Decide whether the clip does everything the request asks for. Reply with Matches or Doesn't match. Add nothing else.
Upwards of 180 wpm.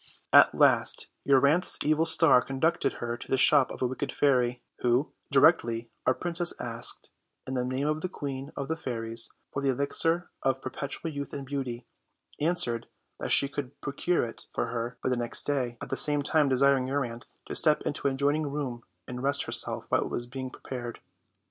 Matches